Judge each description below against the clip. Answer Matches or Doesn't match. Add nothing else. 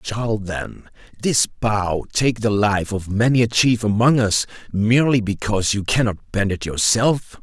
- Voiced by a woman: Doesn't match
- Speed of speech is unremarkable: Matches